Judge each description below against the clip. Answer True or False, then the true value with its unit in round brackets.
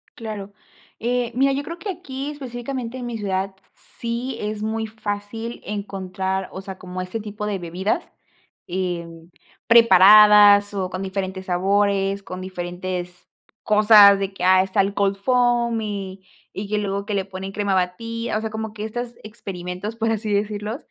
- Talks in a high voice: True (205 Hz)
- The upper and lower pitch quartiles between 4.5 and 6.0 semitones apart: False (3.0 semitones)